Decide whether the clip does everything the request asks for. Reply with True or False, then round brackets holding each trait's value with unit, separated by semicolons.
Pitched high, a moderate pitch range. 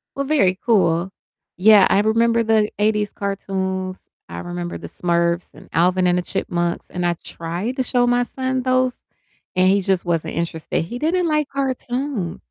False (195 Hz; 6.0 semitones)